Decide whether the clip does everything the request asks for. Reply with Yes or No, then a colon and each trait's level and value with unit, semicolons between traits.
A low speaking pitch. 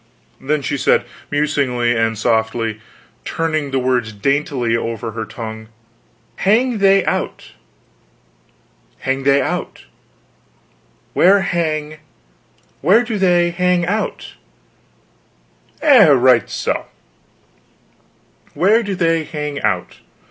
No: medium, 150 Hz